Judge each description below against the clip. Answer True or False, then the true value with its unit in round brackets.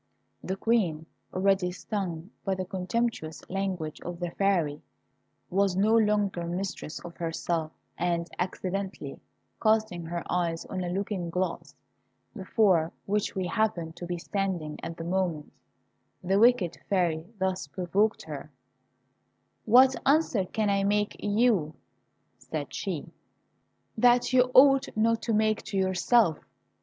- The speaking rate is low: True (130 wpm)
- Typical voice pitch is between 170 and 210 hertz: True (190 Hz)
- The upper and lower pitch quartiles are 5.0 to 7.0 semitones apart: False (3.6 semitones)